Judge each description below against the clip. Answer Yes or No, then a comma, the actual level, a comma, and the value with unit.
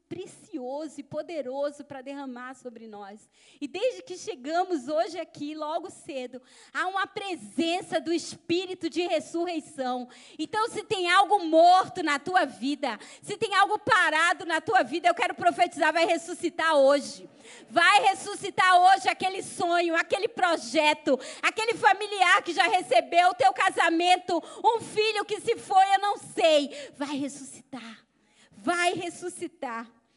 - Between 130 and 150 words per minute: Yes, average, 140 wpm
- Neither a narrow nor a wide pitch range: Yes, average, 4.6 semitones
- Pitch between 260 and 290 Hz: No, very high, 340 Hz